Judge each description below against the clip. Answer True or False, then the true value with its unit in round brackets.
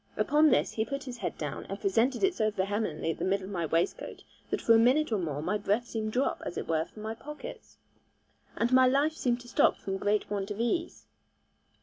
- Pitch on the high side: True (225 Hz)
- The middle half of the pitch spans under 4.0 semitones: False (4.6 semitones)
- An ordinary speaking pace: False (230 wpm)